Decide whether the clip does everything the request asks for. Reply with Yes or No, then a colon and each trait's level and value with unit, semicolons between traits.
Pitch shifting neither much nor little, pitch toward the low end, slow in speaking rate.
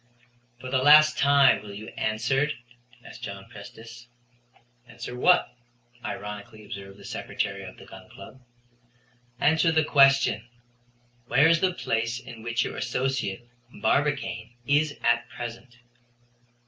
Yes: average, 4.3 semitones; low, 125 Hz; slow, 125 wpm